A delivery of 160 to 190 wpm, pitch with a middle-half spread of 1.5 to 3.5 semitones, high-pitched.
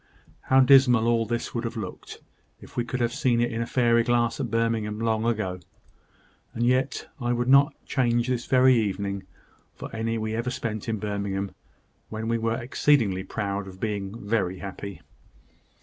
No: average, 175 wpm; narrow, 2.6 semitones; low, 115 Hz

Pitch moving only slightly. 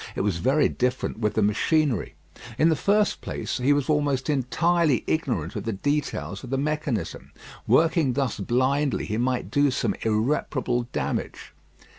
No: average, 4.4 semitones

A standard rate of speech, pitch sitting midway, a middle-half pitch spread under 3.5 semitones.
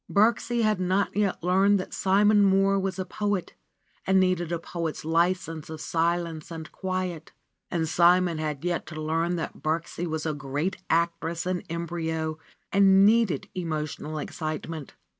Yes: average, 150 wpm; medium, 170 Hz; average, 3.0 semitones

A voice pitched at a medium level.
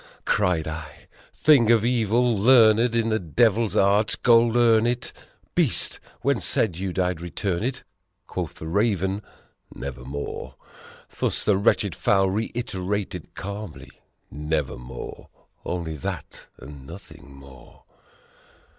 No: low, 100 Hz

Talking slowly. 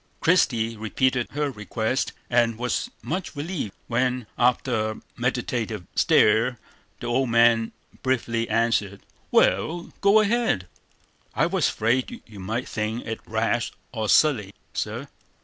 Yes: slow, 125 wpm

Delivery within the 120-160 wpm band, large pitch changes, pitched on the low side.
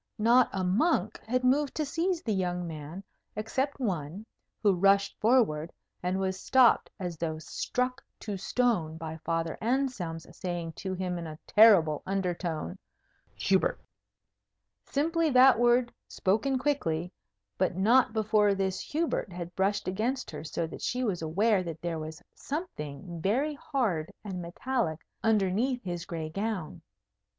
No: average, 140 wpm; wide, 6.5 semitones; high, 195 Hz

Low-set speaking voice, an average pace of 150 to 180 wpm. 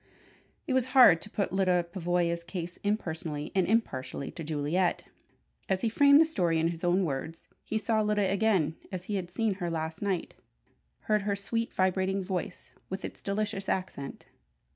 No: medium, 185 Hz; average, 170 wpm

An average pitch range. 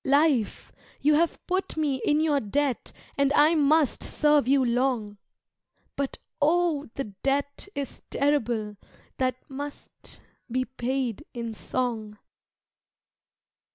Yes: average, 3.4 semitones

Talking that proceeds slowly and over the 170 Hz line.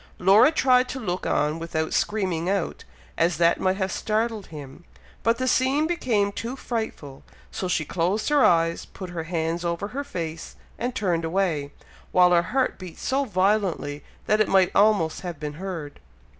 No: average, 170 wpm; medium, 185 Hz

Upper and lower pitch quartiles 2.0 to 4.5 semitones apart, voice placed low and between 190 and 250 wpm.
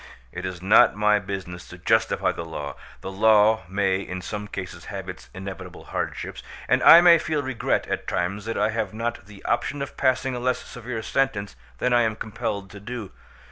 Yes: average, 4.0 semitones; low, 105 Hz; average, 195 wpm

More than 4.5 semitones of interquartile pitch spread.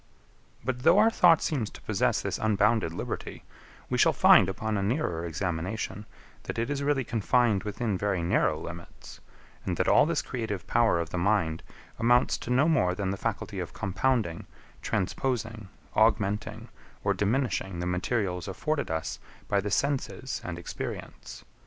Yes: average, 5.3 semitones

